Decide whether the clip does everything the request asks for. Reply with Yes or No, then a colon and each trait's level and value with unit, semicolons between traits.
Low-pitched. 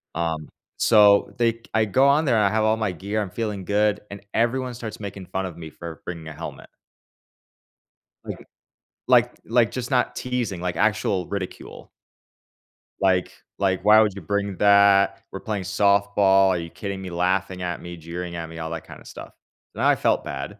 Yes: low, 100 Hz